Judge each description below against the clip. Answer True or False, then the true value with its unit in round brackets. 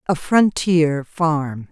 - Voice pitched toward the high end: False (160 Hz)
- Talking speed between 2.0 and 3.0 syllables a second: True (2.6 syllables/s)